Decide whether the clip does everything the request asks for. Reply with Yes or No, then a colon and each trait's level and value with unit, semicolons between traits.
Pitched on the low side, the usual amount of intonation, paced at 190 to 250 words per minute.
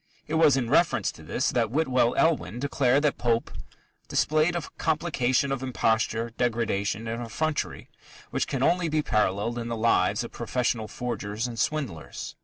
No: low, 125 Hz; average, 4.6 semitones; average, 160 wpm